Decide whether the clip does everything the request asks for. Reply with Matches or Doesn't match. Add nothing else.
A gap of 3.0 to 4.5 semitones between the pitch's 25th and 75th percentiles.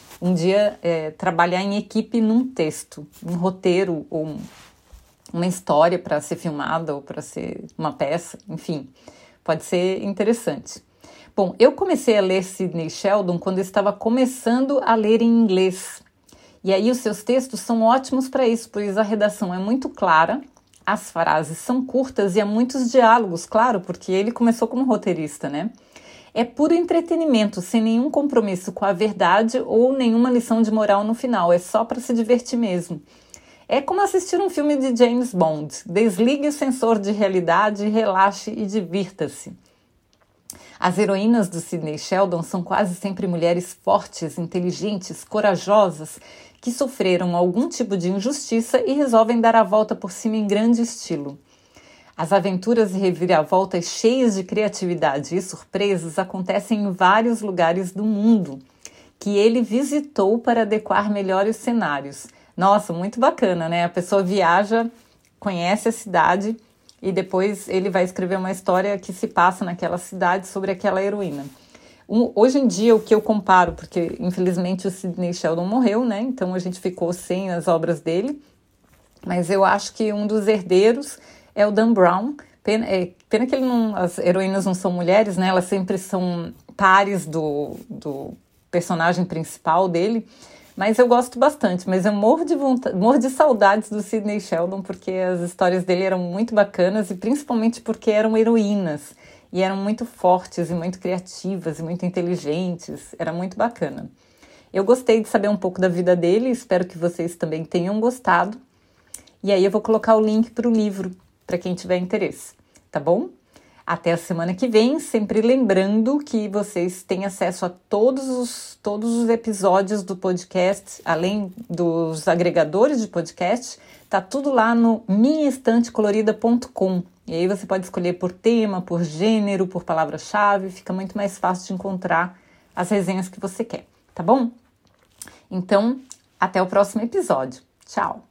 Matches